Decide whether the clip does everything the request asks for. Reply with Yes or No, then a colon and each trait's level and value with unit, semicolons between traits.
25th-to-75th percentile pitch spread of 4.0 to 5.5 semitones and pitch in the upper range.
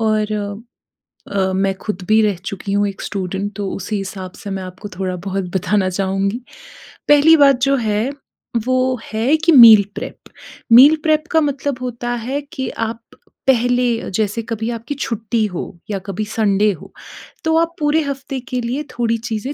Yes: average, 4.6 semitones; high, 225 Hz